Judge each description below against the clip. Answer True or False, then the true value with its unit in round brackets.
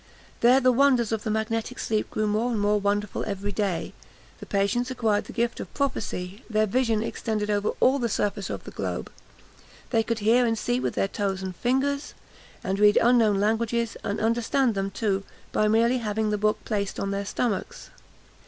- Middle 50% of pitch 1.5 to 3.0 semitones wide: True (2.6 semitones)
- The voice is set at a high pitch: True (220 Hz)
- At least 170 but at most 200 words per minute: True (190 wpm)